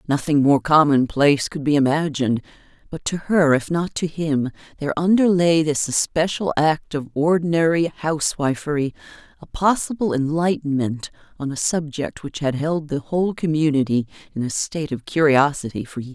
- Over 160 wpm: No, average, 150 wpm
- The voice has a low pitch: No, medium, 150 Hz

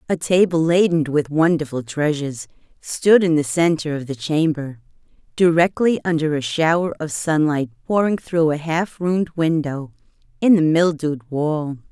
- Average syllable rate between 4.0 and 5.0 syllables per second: Yes, 4.7 syllables/s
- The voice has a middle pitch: Yes, medium, 160 Hz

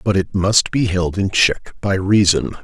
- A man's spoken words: Yes, male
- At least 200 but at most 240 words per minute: Yes, fast, 205 wpm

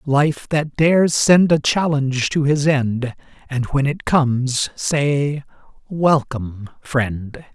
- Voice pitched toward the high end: No, medium, 140 Hz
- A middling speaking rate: No, slow, 125 wpm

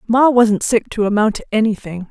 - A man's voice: No, female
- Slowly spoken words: No, average, 200 wpm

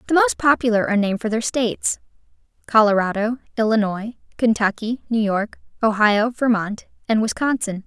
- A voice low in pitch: No, high, 225 Hz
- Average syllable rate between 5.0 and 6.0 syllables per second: Yes, 5.4 syllables/s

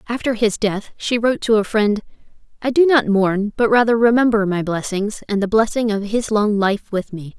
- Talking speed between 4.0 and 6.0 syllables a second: Yes, 5.1 syllables/s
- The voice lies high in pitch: Yes, high, 215 Hz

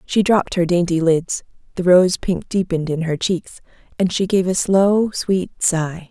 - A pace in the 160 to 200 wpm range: Yes, average, 185 wpm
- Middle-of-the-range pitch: Yes, medium, 180 Hz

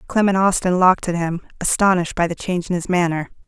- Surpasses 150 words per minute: Yes, fast, 205 wpm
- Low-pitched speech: No, medium, 180 Hz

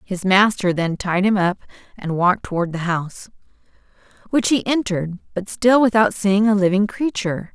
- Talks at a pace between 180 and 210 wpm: No, average, 165 wpm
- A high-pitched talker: Yes, high, 195 Hz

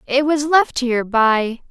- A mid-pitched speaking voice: No, very high, 255 Hz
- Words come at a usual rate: Yes, average, 175 wpm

